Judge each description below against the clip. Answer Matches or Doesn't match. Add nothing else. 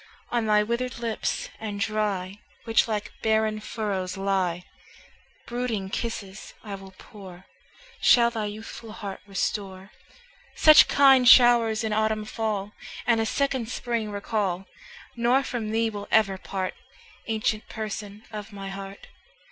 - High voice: Matches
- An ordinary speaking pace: Doesn't match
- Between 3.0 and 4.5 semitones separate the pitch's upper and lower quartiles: Doesn't match